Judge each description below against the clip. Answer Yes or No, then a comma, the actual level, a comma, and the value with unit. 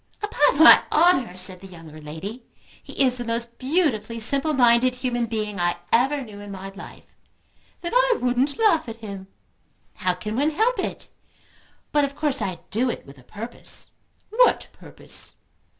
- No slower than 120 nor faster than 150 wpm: No, average, 165 wpm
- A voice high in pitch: Yes, high, 235 Hz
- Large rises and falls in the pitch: Yes, wide, 6.2 semitones